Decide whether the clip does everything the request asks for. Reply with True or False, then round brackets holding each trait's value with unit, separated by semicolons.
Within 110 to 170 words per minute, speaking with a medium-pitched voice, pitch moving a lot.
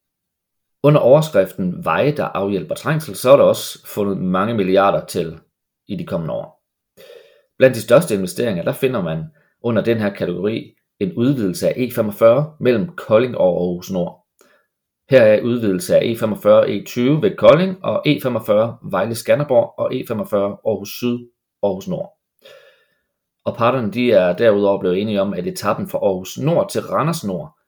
False (160 wpm; 120 Hz; 6.8 semitones)